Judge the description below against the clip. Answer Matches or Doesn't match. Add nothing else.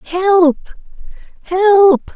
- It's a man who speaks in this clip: Doesn't match